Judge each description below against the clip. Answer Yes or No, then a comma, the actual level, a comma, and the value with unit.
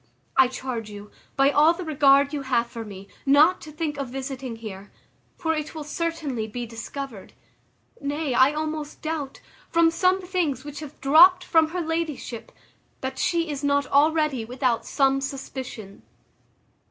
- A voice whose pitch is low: No, very high, 280 Hz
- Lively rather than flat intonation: No, average, 3.6 semitones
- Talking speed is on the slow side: No, average, 155 wpm